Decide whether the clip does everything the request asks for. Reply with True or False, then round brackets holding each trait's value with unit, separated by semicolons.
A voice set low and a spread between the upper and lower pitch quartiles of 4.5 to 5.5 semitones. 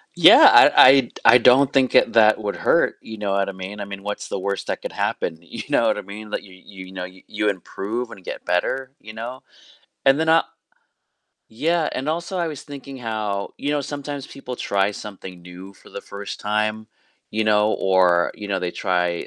True (105 Hz; 5.1 semitones)